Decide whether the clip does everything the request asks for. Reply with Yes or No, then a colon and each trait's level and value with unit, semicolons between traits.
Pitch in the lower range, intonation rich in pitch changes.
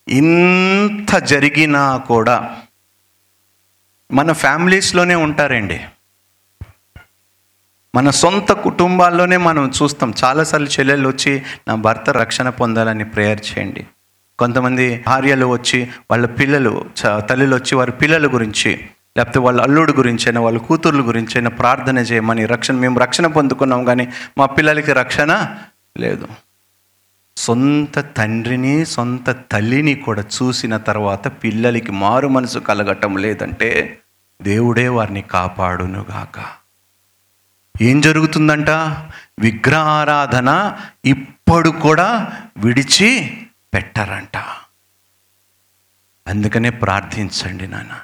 Yes: low, 125 Hz; wide, 5.7 semitones